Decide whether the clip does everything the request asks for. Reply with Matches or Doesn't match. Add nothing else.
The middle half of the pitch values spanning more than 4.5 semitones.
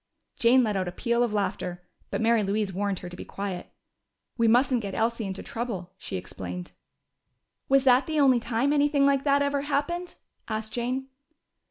Matches